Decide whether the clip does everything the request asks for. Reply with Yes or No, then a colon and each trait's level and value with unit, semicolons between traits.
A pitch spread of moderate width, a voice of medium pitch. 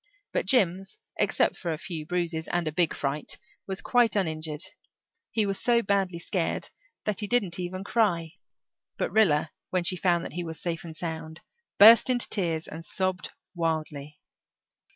Yes: average, 3.4 semitones; medium, 175 Hz